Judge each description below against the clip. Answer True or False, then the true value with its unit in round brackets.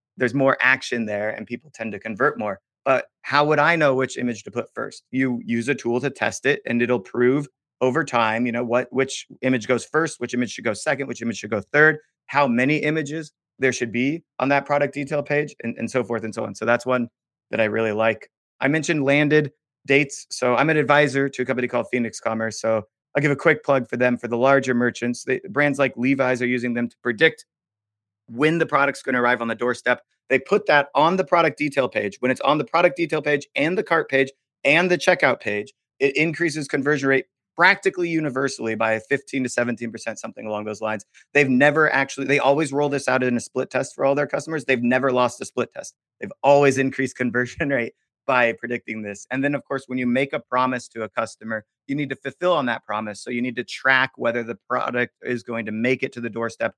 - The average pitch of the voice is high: False (130 Hz)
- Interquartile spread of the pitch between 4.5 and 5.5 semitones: False (3.2 semitones)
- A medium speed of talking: False (235 wpm)